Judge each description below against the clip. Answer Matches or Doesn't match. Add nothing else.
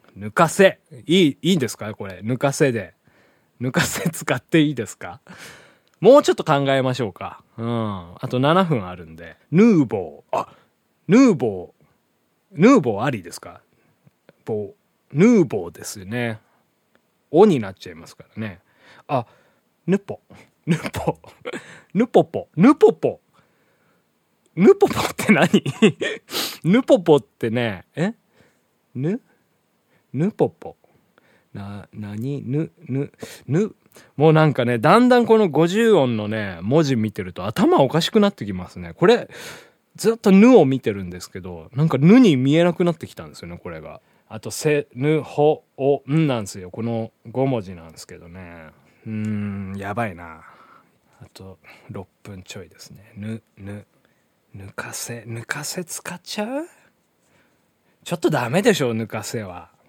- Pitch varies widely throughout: Matches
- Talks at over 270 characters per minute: Doesn't match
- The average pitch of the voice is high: Doesn't match